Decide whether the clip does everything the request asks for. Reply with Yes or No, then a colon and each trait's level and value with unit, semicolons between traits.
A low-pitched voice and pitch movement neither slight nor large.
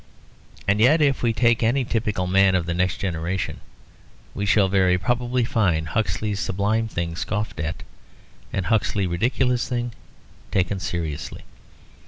Yes: low, 100 Hz; average, 4.3 semitones